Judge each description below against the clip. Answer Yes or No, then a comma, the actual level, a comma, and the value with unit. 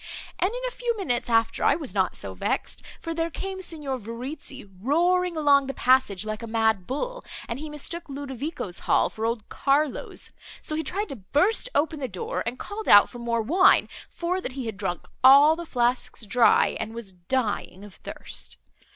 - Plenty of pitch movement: Yes, wide, 6.4 semitones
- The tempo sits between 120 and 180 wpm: No, average, 190 wpm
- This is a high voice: Yes, very high, 270 Hz